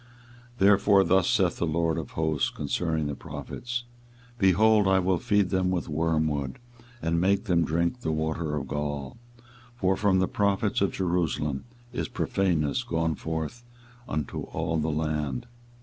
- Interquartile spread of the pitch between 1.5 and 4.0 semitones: Yes, average, 3.7 semitones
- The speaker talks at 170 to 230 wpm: No, average, 150 wpm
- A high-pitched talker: No, very low, 85 Hz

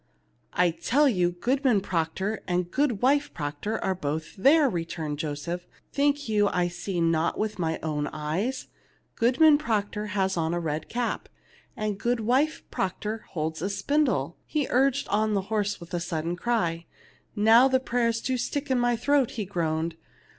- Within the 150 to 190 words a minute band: Yes, average, 160 wpm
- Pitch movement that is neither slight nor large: No, wide, 6.5 semitones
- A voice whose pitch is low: No, high, 205 Hz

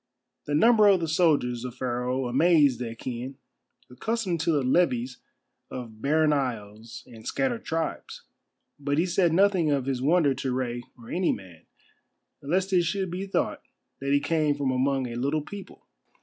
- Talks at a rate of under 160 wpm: No, average, 165 wpm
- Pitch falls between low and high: Yes, medium, 145 Hz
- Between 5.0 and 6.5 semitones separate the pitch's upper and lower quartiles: Yes, wide, 5.4 semitones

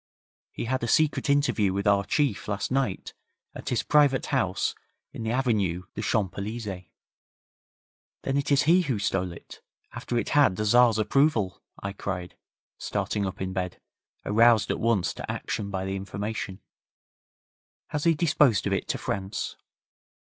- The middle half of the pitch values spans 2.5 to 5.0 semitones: No, wide, 5.4 semitones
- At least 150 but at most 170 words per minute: Yes, average, 160 wpm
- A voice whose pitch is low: Yes, low, 105 Hz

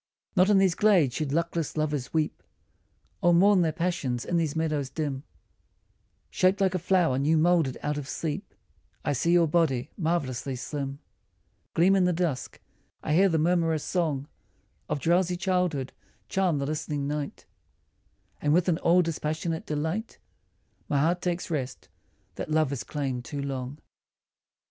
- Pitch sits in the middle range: Yes, medium, 160 Hz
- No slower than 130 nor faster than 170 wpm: Yes, average, 155 wpm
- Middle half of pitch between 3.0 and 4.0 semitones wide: Yes, average, 3.5 semitones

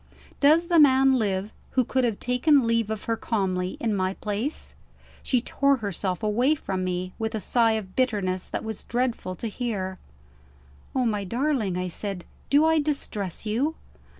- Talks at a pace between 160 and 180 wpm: Yes, average, 170 wpm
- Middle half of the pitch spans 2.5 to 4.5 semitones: No, average, 5.1 semitones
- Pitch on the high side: Yes, high, 225 Hz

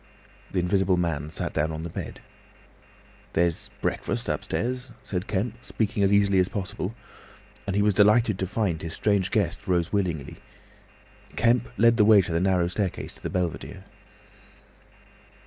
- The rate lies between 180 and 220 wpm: No, average, 155 wpm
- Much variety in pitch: No, average, 3.3 semitones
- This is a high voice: No, very low, 95 Hz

